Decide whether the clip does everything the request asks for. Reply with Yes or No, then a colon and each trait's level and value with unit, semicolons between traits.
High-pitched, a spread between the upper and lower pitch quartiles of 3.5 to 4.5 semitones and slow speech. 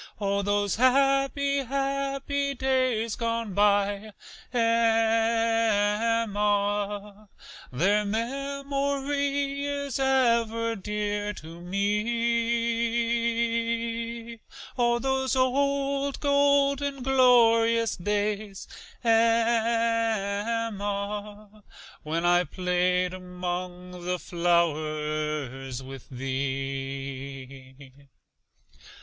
Yes: high, 225 Hz; average, 4.1 semitones; slow, 65 wpm